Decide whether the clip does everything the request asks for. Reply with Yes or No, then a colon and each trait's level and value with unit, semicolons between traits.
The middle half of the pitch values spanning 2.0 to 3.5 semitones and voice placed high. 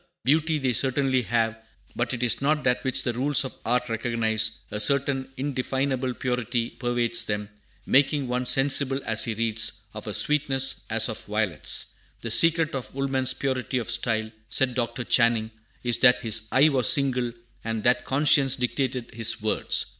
No: average, 2.9 semitones; low, 125 Hz